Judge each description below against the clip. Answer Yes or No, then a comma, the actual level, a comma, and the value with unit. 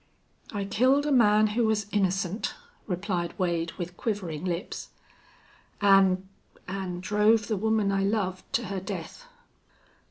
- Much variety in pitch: No, average, 2.7 semitones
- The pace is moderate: No, slow, 130 wpm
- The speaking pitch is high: Yes, high, 195 Hz